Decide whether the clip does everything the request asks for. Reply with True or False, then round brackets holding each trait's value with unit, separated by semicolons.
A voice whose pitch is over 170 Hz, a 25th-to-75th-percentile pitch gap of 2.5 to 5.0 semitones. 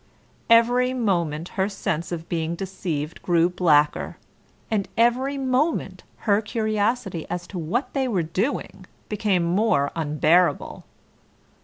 False (190 Hz; 5.5 semitones)